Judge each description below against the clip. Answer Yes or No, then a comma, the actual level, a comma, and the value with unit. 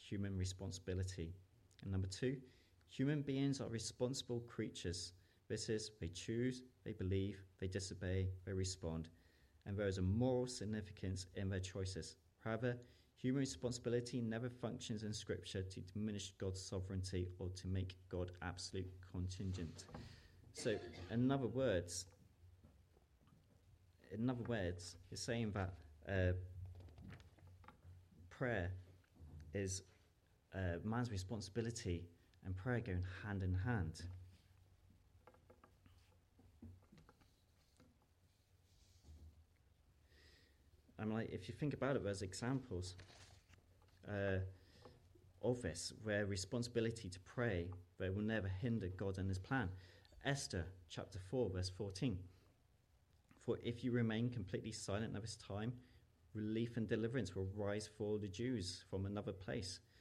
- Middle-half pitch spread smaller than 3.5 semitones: No, average, 3.8 semitones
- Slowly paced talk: Yes, slow, 115 wpm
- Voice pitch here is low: Yes, very low, 95 Hz